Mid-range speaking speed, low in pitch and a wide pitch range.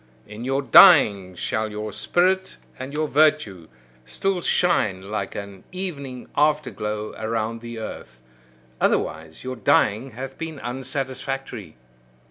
No: slow, 120 wpm; low, 125 Hz; wide, 5.9 semitones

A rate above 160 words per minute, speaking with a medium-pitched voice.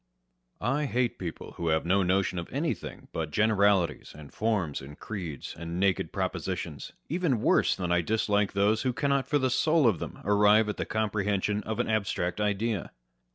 No: average, 175 wpm; low, 105 Hz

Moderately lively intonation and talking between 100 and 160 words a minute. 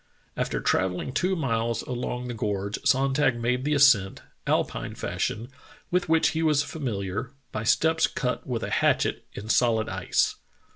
Yes: average, 4.5 semitones; average, 150 wpm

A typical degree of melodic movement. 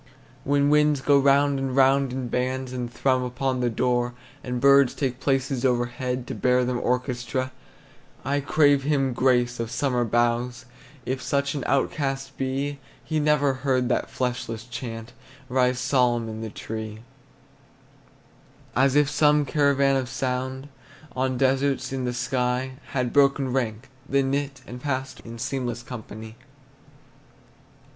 No: narrow, 2.0 semitones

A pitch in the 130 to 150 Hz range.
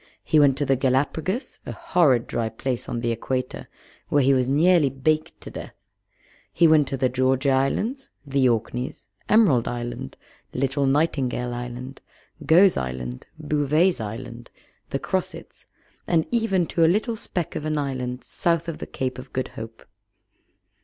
Yes: low, 135 Hz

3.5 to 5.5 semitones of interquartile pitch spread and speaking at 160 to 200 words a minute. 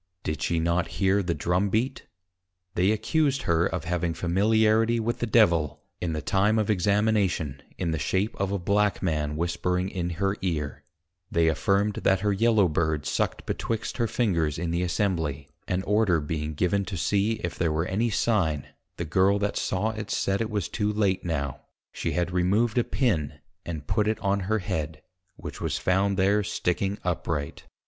Yes: average, 4.0 semitones; average, 180 wpm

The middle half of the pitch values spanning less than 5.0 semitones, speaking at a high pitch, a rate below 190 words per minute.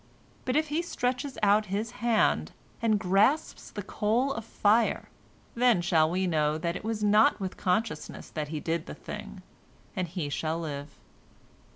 No: wide, 5.4 semitones; high, 205 Hz; average, 165 wpm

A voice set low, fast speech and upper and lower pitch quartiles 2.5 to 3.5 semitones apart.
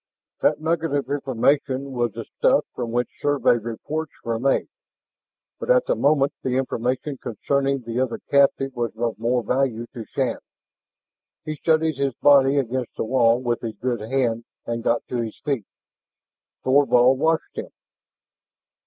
No: low, 130 Hz; average, 155 wpm; average, 3.0 semitones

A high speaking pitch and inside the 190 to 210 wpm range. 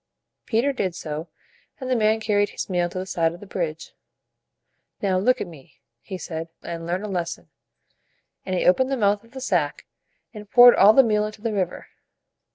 Yes: high, 200 Hz; average, 195 wpm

